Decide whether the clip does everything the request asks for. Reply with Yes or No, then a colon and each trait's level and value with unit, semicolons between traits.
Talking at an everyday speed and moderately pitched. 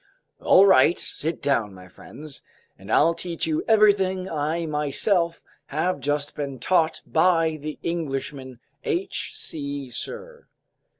No: slow, 125 wpm; medium, 160 Hz